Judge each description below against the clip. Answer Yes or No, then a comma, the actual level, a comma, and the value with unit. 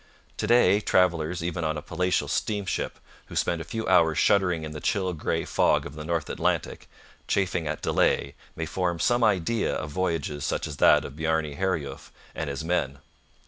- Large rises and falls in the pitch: No, average, 3.2 semitones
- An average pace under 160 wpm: No, average, 185 wpm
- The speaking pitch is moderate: No, very low, 85 Hz